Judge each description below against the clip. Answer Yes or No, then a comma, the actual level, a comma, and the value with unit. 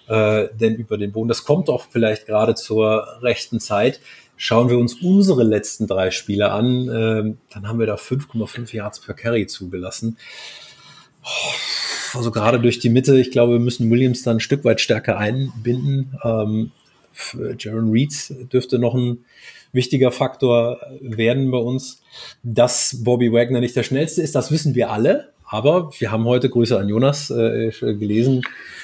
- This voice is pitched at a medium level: No, low, 120 Hz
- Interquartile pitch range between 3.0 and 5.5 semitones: No, narrow, 2.4 semitones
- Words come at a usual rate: Yes, average, 155 wpm